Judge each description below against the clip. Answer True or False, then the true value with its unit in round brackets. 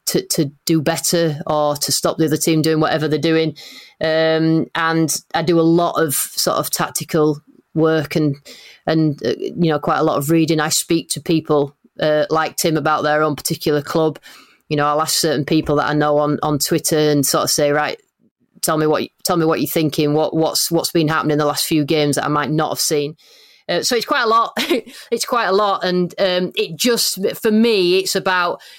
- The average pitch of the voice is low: False (160 Hz)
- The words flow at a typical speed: False (220 wpm)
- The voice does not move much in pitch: True (2.0 semitones)